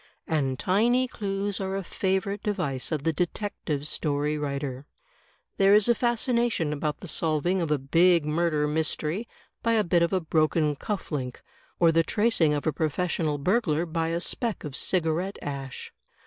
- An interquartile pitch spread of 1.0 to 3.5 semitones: No, average, 4.6 semitones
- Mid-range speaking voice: Yes, medium, 165 Hz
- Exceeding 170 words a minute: No, average, 165 wpm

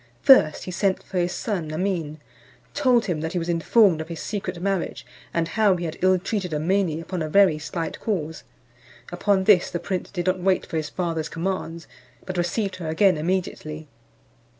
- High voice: No, medium, 180 Hz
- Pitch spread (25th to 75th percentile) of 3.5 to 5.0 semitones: No, average, 2.9 semitones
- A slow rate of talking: No, average, 185 wpm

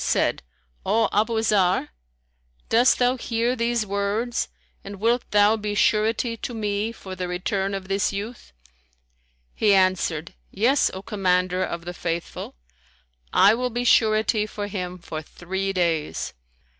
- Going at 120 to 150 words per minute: Yes, average, 140 wpm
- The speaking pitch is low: No, high, 205 Hz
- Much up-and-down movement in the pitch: No, average, 3.3 semitones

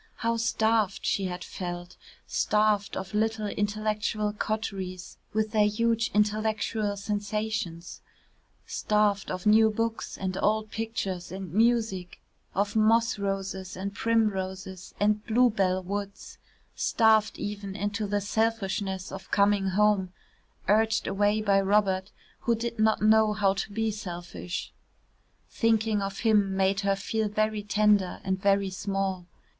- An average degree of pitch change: No, narrow, 2.1 semitones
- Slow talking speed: Yes, slow, 130 wpm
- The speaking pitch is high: Yes, high, 205 Hz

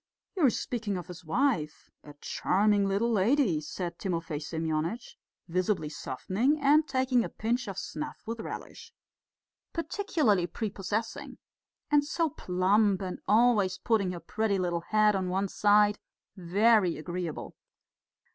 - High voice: Yes, high, 205 Hz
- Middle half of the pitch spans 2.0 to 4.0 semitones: No, average, 4.7 semitones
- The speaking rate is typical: No, slow, 130 wpm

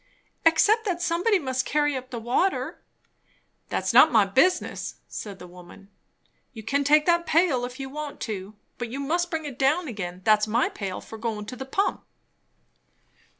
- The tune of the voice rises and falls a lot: Yes, wide, 6.7 semitones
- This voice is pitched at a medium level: No, very high, 265 Hz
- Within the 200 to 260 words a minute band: No, average, 175 wpm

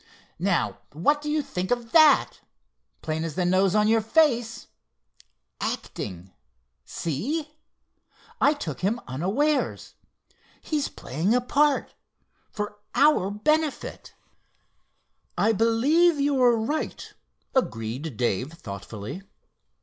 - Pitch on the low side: No, high, 225 Hz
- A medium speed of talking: No, slow, 100 wpm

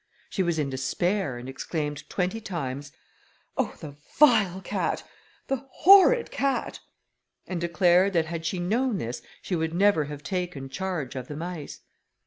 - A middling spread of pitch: Yes, average, 5.0 semitones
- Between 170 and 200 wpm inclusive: No, average, 150 wpm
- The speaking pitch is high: No, medium, 175 Hz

